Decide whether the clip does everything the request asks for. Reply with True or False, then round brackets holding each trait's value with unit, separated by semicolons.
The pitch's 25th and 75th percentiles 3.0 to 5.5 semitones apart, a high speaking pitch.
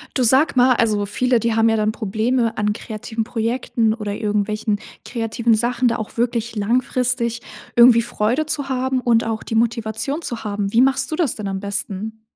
False (2.5 semitones; 230 Hz)